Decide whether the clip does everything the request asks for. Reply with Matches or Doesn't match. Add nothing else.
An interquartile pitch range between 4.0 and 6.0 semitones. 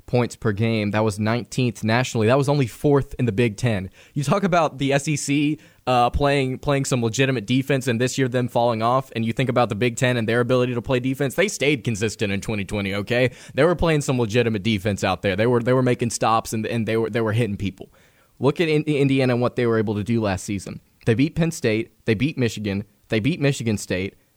Doesn't match